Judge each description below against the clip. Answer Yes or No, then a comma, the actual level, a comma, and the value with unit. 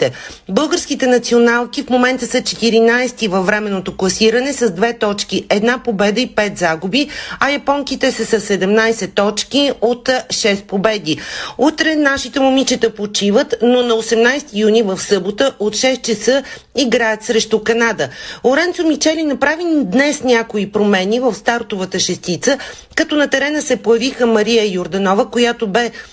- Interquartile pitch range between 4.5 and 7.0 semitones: No, average, 3.8 semitones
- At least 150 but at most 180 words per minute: No, average, 140 wpm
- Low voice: No, high, 235 Hz